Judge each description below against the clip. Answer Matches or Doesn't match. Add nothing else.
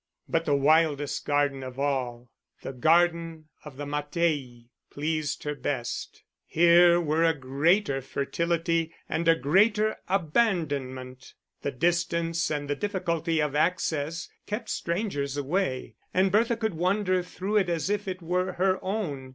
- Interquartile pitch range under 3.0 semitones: Doesn't match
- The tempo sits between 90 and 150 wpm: Matches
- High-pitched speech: Doesn't match